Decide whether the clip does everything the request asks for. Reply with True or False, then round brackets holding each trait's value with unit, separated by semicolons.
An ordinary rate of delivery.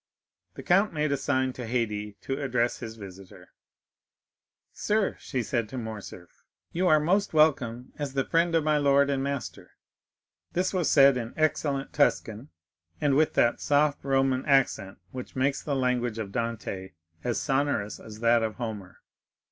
True (160 wpm)